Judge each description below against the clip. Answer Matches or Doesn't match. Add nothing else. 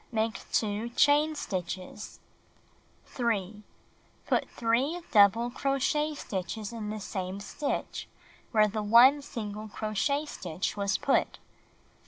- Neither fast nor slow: Doesn't match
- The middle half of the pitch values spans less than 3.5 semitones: Doesn't match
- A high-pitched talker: Matches